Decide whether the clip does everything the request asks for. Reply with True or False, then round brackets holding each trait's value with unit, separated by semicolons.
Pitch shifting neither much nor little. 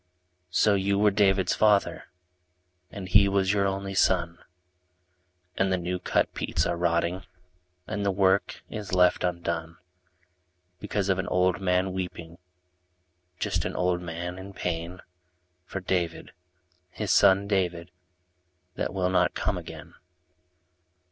False (1.8 semitones)